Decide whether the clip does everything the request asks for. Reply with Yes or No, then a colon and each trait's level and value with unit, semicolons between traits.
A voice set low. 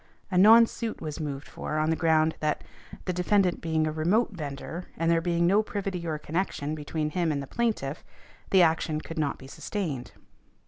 No: medium, 165 Hz